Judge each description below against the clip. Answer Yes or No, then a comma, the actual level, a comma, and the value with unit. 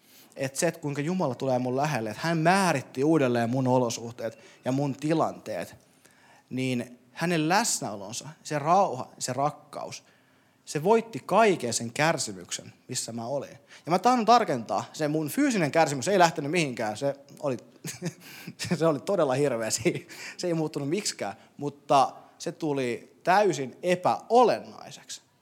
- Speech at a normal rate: Yes, average, 135 wpm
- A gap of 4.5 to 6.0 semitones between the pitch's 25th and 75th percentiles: Yes, average, 5.0 semitones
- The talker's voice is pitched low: No, medium, 150 Hz